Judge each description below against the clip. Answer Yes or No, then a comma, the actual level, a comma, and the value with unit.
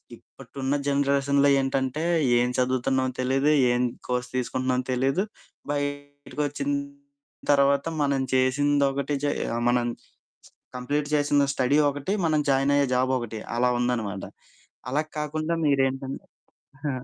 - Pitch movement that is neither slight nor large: No, narrow, 1.9 semitones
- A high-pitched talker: No, low, 135 Hz